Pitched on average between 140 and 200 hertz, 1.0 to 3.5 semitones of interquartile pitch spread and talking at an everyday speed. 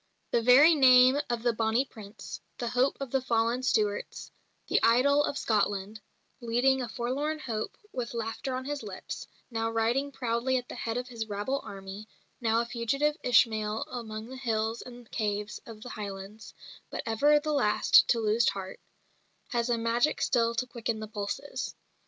No: high, 235 Hz; average, 2.7 semitones; average, 170 wpm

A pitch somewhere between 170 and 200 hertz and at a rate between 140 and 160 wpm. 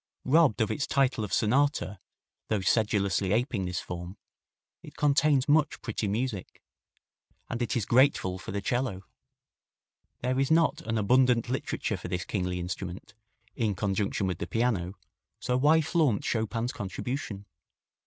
No: low, 115 Hz; average, 145 wpm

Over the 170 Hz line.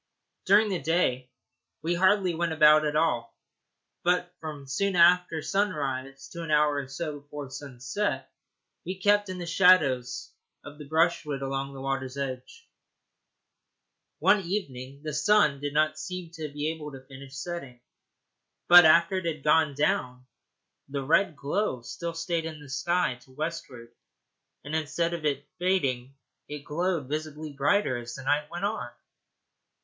No: medium, 150 Hz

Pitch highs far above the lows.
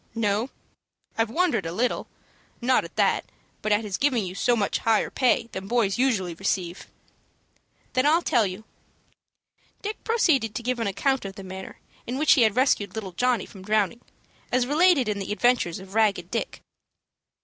No: average, 4.3 semitones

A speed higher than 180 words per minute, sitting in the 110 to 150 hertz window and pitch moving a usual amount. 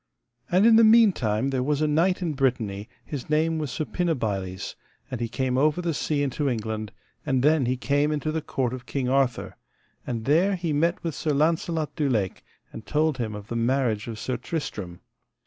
Yes: average, 195 wpm; medium, 140 Hz; average, 4.9 semitones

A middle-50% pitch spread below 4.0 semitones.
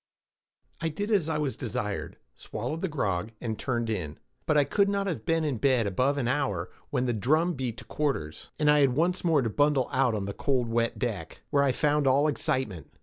No: average, 4.8 semitones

